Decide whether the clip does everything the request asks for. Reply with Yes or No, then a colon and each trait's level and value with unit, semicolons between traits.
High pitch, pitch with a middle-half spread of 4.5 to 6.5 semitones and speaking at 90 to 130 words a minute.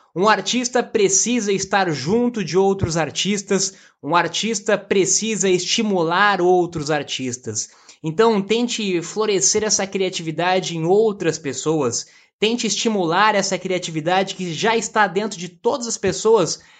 No: high, 195 Hz; average, 3.5 semitones; slow, 120 wpm